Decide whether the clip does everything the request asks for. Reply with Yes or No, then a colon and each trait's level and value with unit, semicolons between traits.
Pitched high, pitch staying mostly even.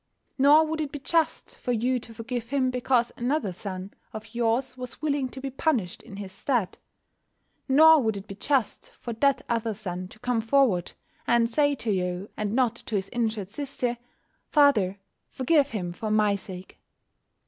No: high, 235 Hz; average, 4.7 semitones